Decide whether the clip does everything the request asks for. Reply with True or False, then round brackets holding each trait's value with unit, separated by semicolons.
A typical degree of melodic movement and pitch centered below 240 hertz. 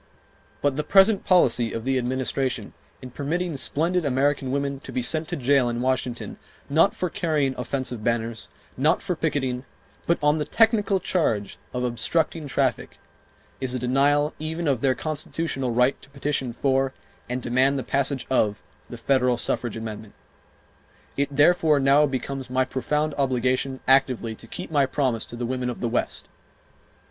True (3.0 semitones; 135 Hz)